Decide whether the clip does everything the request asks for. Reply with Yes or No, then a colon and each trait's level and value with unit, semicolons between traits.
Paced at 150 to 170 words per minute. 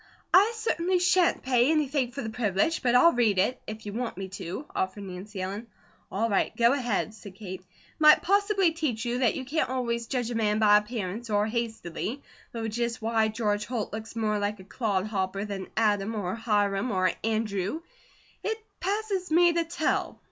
No: average, 190 wpm